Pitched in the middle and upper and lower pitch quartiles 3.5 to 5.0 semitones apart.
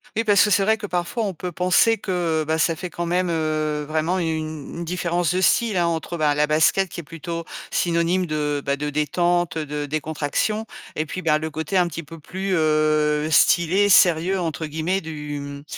No: medium, 165 Hz; average, 2.9 semitones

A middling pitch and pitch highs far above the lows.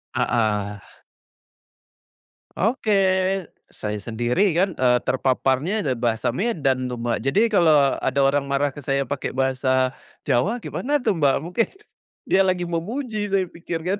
Yes: medium, 145 Hz; wide, 6.9 semitones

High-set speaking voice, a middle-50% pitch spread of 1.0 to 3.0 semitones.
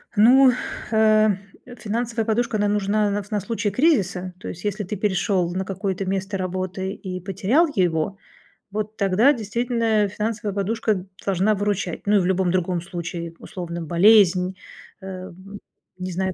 Yes: high, 195 Hz; average, 2.7 semitones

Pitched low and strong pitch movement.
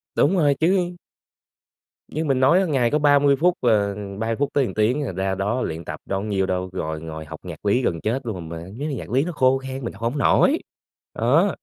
Yes: low, 125 Hz; wide, 6.6 semitones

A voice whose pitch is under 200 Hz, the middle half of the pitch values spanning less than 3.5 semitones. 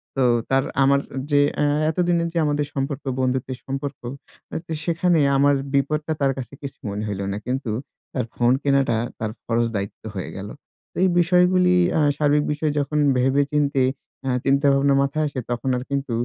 Yes: medium, 140 Hz; narrow, 2.5 semitones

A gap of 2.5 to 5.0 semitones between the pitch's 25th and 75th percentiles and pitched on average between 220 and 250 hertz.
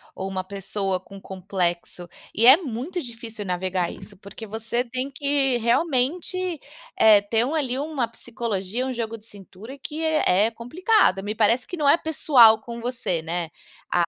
No: wide, 5.4 semitones; high, 230 Hz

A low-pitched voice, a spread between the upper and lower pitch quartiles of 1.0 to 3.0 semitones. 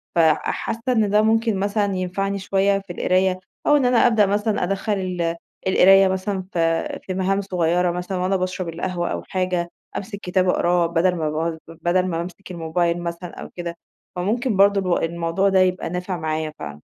No: medium, 185 Hz; narrow, 2.4 semitones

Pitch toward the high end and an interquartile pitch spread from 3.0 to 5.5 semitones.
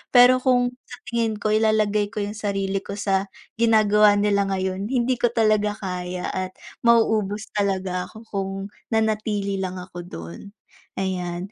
No: high, 205 Hz; narrow, 2.4 semitones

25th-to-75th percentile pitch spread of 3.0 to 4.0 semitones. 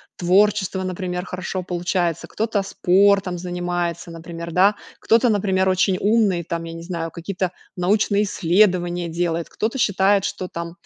No: narrow, 2.5 semitones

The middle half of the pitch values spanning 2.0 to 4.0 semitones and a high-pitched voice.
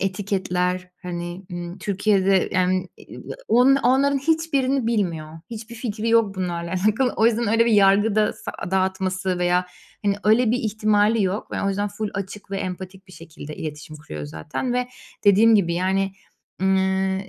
Yes: average, 3.2 semitones; high, 195 Hz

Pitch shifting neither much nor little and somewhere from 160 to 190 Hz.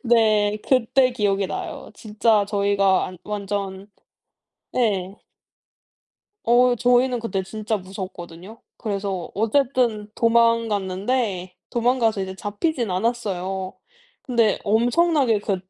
No: average, 3.3 semitones; high, 210 Hz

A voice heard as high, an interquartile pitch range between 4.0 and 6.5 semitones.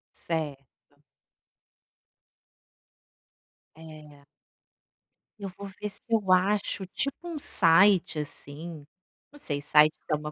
No: medium, 160 Hz; average, 5.0 semitones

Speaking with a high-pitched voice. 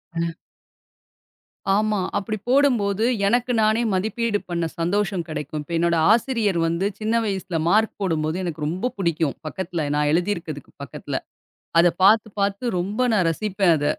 Yes: high, 195 Hz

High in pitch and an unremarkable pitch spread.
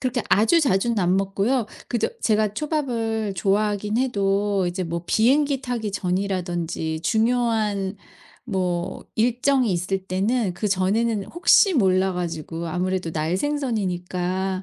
Yes: high, 200 Hz; average, 4.2 semitones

